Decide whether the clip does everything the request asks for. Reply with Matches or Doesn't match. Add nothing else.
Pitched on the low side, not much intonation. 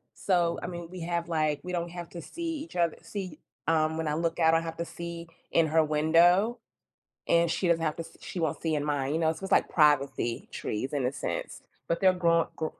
Doesn't match